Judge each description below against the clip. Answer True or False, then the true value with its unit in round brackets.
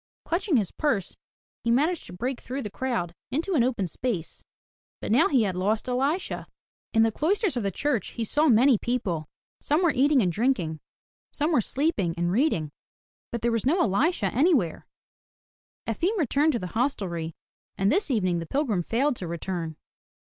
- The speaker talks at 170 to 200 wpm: True (175 wpm)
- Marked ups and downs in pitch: True (7.4 semitones)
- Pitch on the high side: True (240 Hz)